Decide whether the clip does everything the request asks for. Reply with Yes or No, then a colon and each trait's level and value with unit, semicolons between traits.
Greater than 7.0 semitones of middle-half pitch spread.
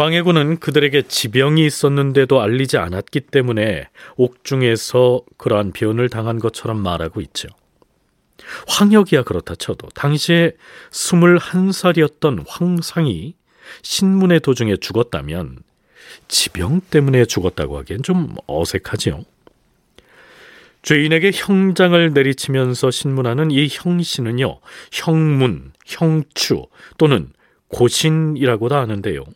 No: wide, 5.6 semitones